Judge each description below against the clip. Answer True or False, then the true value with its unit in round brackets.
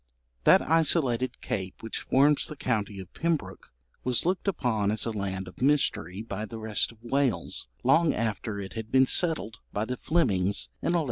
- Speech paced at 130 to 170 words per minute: False (185 wpm)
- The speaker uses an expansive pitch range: True (5.8 semitones)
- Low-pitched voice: True (115 Hz)